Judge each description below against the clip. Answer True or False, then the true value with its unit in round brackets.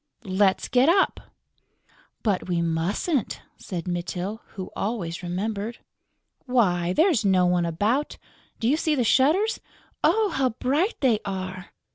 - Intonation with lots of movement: True (6.5 semitones)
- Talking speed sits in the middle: False (130 wpm)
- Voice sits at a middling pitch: False (210 Hz)